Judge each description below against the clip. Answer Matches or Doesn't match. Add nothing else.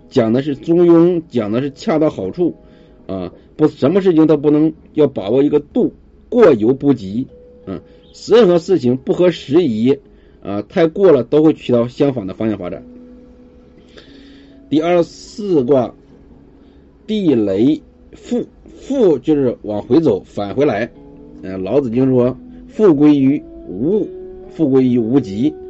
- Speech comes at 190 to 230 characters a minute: Matches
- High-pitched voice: Doesn't match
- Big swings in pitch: Matches